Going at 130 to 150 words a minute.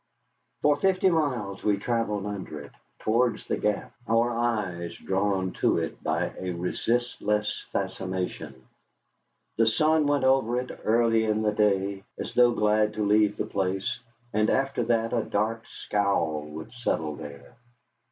Yes: average, 145 wpm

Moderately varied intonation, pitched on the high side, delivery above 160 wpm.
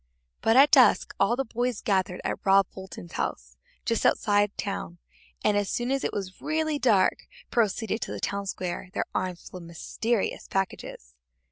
Yes: average, 4.1 semitones; high, 205 Hz; average, 170 wpm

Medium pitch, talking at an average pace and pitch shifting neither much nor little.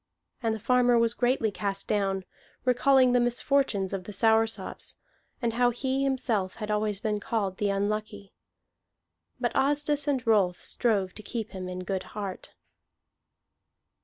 No: high, 220 Hz; average, 145 wpm; average, 3.8 semitones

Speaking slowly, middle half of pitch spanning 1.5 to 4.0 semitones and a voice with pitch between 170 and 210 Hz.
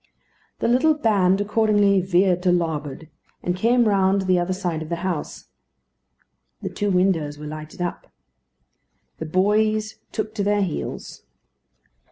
No: average, 145 wpm; average, 3.1 semitones; high, 190 Hz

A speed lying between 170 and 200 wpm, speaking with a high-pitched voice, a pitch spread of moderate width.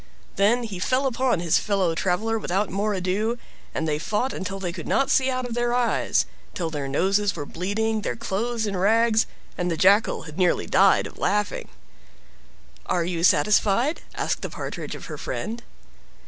Yes: average, 175 wpm; high, 205 Hz; average, 4.3 semitones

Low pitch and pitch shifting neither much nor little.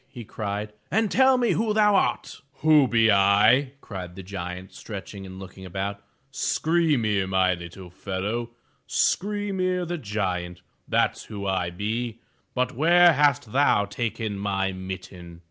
No: low, 105 Hz; wide, 7.3 semitones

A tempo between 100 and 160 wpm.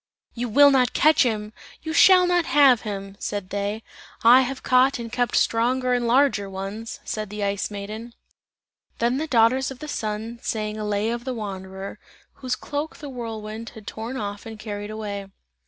No: average, 180 wpm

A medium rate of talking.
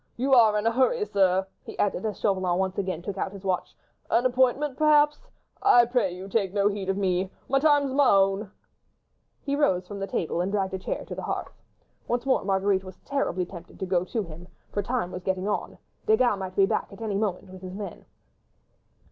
No: fast, 215 wpm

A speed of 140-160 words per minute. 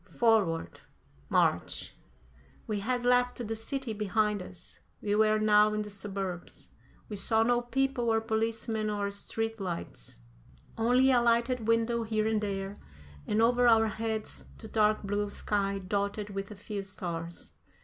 Yes: average, 150 wpm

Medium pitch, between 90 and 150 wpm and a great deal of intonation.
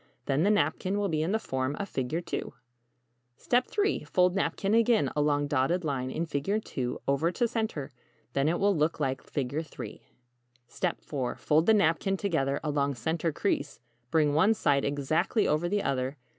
No: medium, 155 Hz; average, 170 wpm; wide, 5.8 semitones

